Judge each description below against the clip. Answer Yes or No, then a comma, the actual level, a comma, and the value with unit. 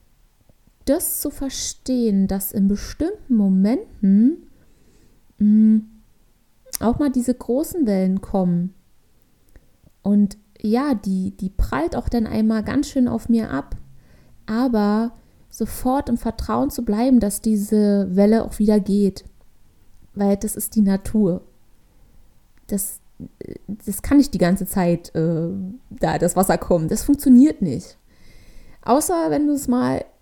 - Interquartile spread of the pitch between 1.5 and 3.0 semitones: No, average, 4.3 semitones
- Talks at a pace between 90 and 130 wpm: Yes, slow, 125 wpm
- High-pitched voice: Yes, high, 215 Hz